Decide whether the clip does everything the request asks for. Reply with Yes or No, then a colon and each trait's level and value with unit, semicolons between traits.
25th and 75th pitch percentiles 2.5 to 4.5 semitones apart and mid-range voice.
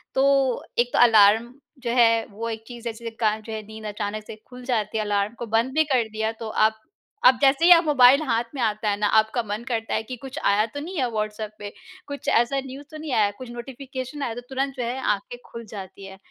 No: average, 3.3 semitones; high, 230 Hz